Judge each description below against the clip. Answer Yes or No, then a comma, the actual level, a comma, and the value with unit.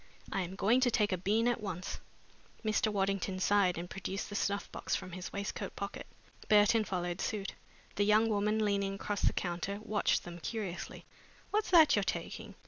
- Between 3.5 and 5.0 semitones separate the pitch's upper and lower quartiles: No, narrow, 2.4 semitones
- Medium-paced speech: Yes, average, 180 wpm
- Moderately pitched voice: No, high, 200 Hz